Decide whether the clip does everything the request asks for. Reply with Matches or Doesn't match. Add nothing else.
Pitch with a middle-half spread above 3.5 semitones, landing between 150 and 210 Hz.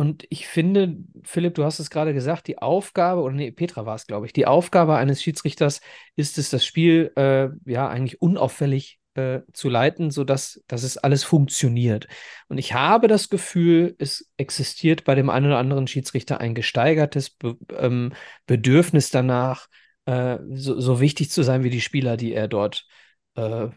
Doesn't match